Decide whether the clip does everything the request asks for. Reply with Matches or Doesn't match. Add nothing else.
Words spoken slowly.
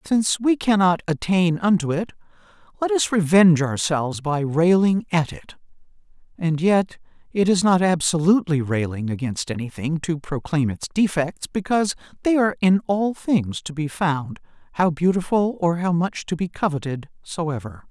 Doesn't match